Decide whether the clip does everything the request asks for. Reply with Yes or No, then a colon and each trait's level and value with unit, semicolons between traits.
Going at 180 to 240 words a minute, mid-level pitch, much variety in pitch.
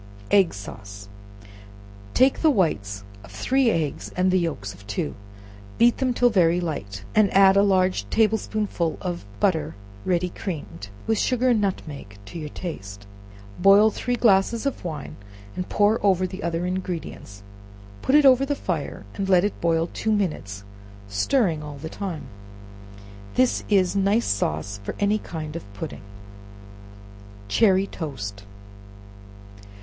No: average, 145 wpm; medium, 180 Hz; wide, 6.6 semitones